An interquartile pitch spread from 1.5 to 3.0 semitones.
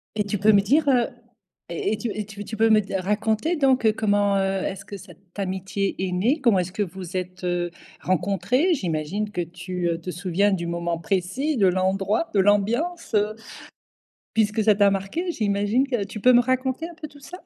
No: average, 3.8 semitones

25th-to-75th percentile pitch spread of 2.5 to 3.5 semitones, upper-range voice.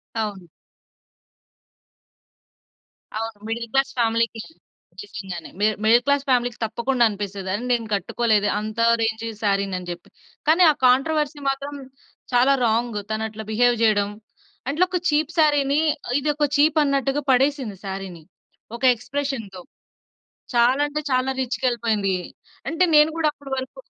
No: average, 4.6 semitones; high, 240 Hz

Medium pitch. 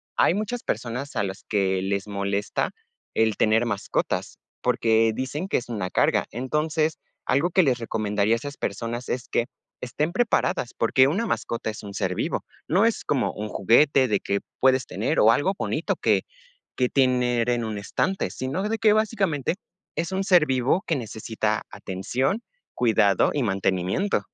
No: low, 120 Hz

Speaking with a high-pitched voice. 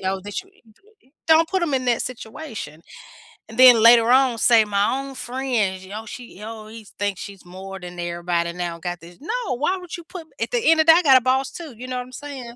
Yes: high, 240 Hz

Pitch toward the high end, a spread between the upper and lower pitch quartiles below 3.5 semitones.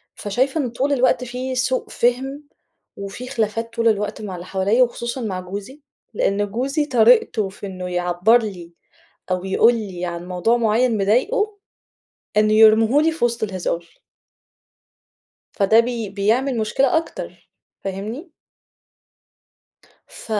No: high, 225 Hz; average, 4.2 semitones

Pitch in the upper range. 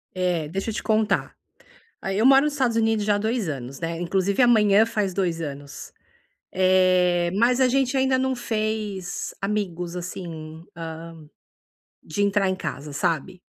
Yes: high, 195 Hz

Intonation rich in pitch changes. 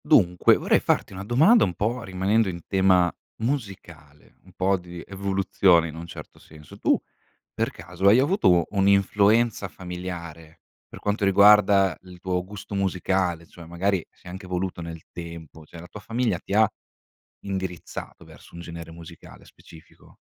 No: average, 2.7 semitones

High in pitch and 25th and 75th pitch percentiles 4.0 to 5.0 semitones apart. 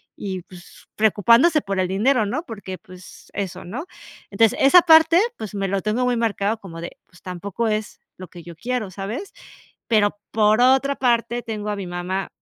Yes: high, 210 Hz; average, 4.4 semitones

